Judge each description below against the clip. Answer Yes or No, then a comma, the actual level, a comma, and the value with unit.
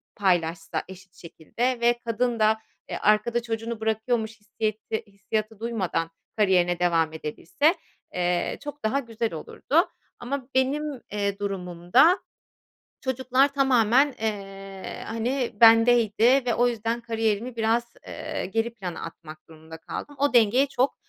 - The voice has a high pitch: Yes, high, 225 Hz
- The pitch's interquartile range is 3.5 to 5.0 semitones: Yes, average, 3.9 semitones